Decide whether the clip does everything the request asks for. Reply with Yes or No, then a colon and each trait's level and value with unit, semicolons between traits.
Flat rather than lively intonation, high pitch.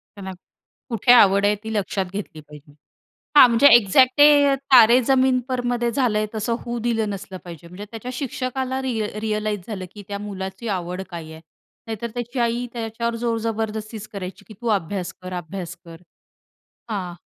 No: average, 4.0 semitones; high, 215 Hz